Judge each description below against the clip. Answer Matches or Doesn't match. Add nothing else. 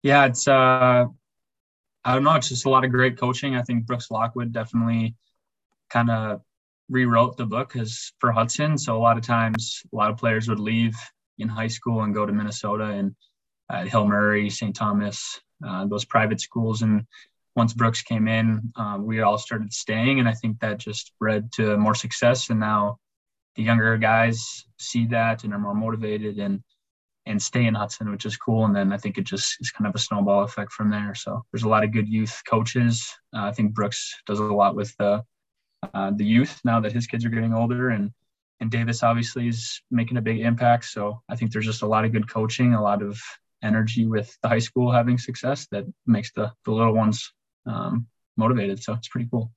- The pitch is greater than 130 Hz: Doesn't match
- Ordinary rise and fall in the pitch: Doesn't match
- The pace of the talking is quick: Matches